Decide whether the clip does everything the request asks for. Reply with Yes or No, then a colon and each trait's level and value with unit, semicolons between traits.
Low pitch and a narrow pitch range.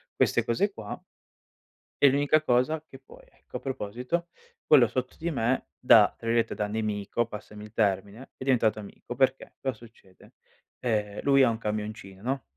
No: low, 120 Hz; average, 4.0 semitones